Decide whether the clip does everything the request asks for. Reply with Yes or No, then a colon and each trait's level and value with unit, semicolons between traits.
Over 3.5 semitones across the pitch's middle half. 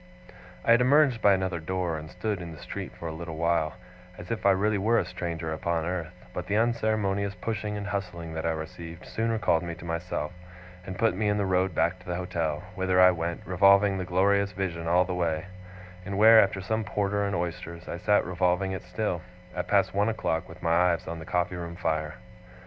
No: average, 3.0 semitones